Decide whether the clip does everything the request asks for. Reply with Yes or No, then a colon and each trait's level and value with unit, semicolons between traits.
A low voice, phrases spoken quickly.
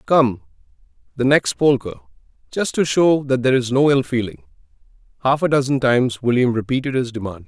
No: low, 130 Hz; average, 160 wpm